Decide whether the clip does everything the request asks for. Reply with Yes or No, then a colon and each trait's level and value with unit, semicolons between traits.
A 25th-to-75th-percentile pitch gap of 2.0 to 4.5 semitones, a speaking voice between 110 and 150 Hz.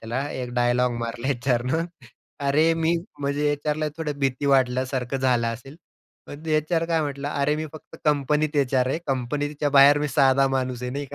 Yes: average, 2.7 semitones; medium, 140 Hz